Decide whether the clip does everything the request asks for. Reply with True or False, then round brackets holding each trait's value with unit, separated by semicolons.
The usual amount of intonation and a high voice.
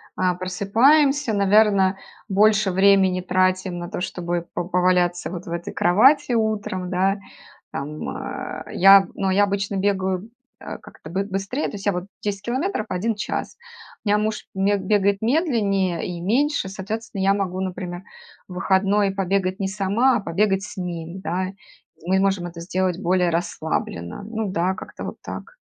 False (2.2 semitones; 195 Hz)